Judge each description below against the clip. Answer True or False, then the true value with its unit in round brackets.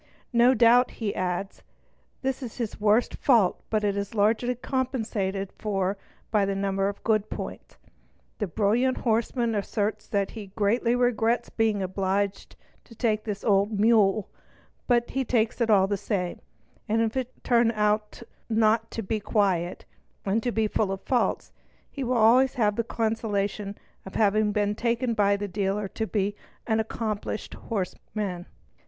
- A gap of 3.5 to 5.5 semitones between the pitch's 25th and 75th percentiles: False (2.5 semitones)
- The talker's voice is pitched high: True (215 Hz)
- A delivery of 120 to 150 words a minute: False (160 wpm)